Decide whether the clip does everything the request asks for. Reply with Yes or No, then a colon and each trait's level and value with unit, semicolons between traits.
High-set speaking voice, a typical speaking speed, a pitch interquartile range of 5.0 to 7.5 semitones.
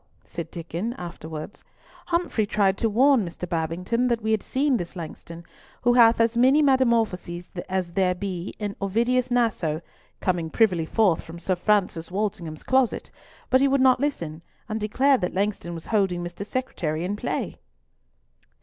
Yes: high, 200 Hz; average, 160 wpm; wide, 5.6 semitones